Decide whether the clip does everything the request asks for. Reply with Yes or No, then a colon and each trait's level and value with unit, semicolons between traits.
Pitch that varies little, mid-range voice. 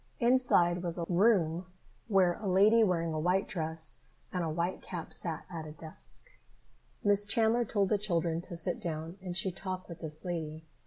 No: average, 3.1 semitones; medium, 175 Hz